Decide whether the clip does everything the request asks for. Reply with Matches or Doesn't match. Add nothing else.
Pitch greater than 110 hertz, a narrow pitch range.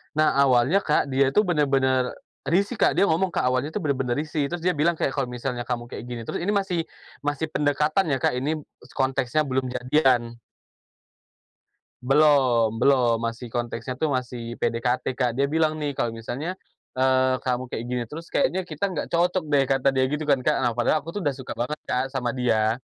Doesn't match